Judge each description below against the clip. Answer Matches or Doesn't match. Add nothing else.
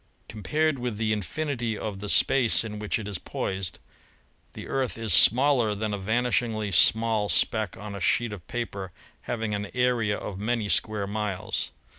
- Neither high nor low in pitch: Doesn't match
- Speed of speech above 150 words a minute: Matches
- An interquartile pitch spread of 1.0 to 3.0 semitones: Matches